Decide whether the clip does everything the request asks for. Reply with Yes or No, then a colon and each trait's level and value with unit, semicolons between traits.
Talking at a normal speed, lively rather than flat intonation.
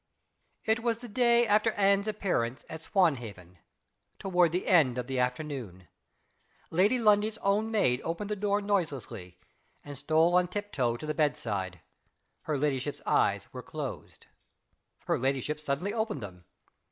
Yes: average, 145 wpm; wide, 8.4 semitones